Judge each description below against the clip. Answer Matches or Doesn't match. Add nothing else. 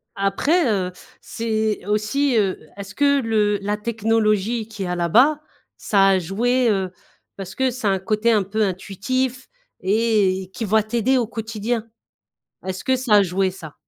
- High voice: Matches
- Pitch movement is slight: Doesn't match